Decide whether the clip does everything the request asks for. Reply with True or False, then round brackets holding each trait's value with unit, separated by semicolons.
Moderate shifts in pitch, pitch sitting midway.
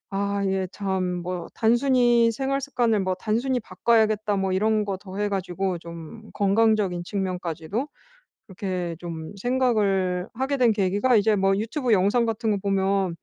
False (3.4 semitones; 200 Hz)